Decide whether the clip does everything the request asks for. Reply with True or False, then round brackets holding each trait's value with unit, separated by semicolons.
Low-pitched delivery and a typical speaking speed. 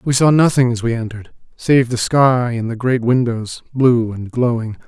True (120 Hz; 195 wpm)